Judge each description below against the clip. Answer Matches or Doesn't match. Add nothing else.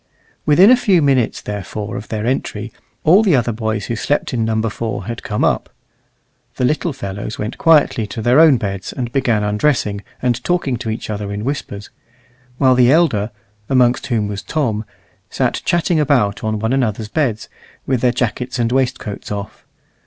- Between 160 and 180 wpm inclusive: Matches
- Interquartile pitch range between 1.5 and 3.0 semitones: Doesn't match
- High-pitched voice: Doesn't match